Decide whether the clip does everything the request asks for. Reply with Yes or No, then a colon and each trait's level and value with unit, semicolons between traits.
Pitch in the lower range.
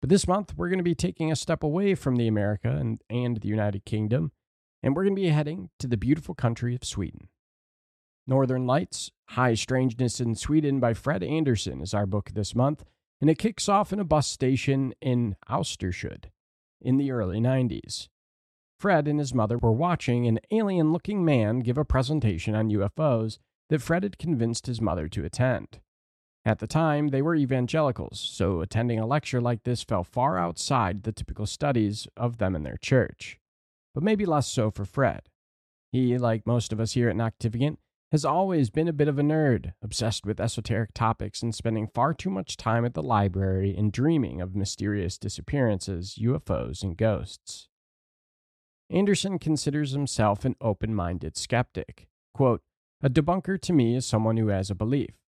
Yes: low, 120 Hz